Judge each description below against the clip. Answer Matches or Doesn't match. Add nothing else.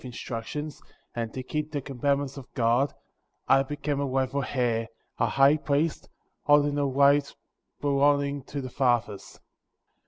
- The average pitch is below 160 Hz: Matches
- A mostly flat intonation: Matches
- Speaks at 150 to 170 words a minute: Doesn't match